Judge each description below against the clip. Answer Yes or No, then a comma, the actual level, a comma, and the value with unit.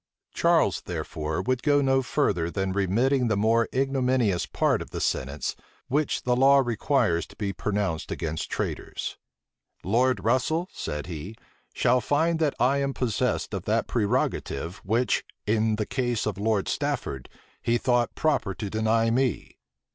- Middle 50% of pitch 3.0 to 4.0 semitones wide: No, average, 5.0 semitones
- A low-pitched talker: Yes, low, 115 Hz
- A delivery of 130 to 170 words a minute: Yes, average, 150 wpm